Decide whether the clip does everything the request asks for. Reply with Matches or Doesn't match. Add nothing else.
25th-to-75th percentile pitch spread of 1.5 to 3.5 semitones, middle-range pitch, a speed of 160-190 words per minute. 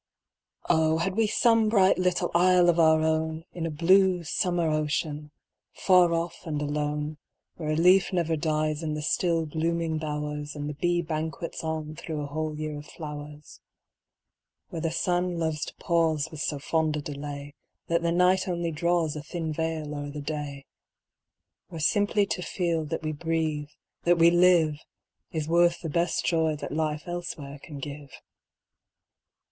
Matches